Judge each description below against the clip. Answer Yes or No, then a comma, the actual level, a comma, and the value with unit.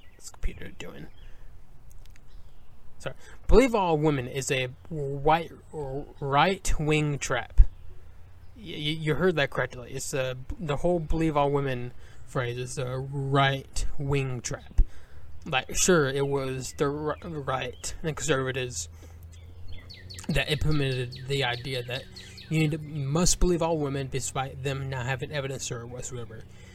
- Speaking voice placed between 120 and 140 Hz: Yes, low, 135 Hz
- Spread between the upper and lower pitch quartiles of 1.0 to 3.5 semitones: No, average, 4.7 semitones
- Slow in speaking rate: Yes, slow, 130 wpm